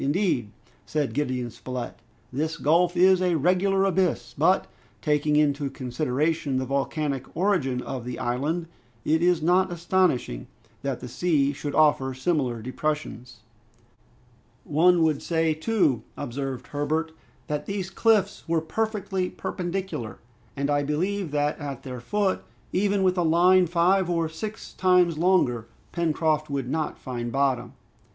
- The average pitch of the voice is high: No, medium, 155 Hz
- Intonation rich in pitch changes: No, average, 4.8 semitones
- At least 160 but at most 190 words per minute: No, slow, 135 wpm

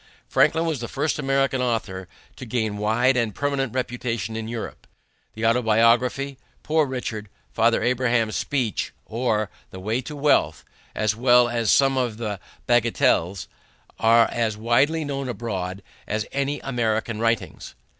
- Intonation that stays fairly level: No, average, 3.2 semitones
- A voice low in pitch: Yes, low, 120 Hz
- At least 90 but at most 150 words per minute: Yes, average, 145 wpm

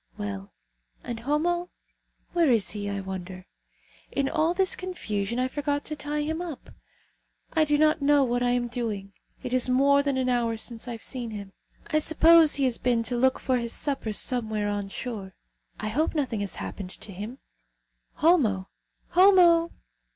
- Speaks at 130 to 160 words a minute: No, average, 175 wpm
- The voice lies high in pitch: Yes, very high, 250 Hz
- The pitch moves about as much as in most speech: No, wide, 5.9 semitones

